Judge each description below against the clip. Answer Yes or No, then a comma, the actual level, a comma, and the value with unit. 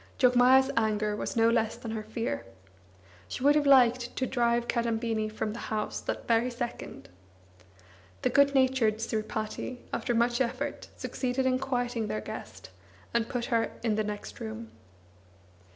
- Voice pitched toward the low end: No, high, 235 Hz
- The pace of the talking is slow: No, average, 150 wpm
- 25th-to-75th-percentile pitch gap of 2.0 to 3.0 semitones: Yes, narrow, 2.4 semitones